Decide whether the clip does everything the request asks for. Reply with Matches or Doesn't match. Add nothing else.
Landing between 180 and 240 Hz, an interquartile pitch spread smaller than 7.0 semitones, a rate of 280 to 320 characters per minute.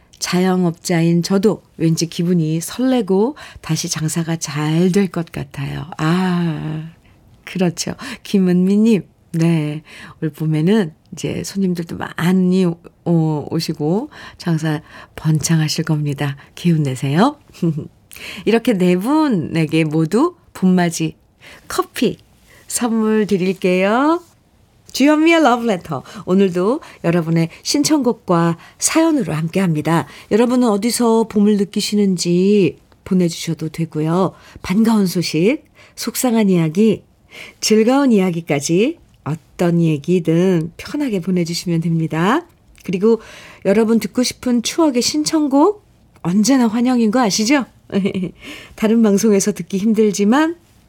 Doesn't match